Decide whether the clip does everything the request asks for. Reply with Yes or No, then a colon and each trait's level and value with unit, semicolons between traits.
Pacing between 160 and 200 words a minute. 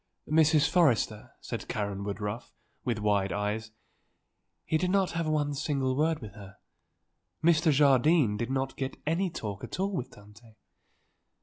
No: average, 145 wpm